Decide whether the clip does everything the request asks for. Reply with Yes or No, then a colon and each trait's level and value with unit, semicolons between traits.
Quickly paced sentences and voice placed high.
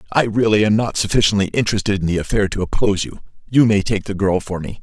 No: fast, 235 wpm; low, 100 Hz